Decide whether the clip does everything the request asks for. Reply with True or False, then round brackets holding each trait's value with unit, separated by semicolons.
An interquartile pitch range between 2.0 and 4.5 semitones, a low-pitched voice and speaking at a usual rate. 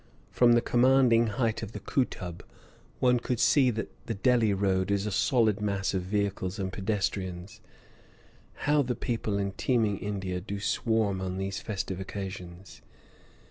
True (3.4 semitones; 100 Hz; 150 wpm)